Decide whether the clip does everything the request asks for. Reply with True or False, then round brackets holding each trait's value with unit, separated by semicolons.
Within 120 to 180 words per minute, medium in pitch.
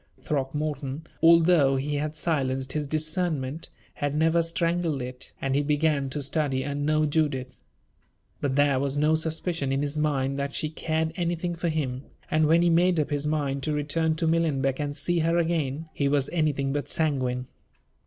True (175 wpm; 150 Hz)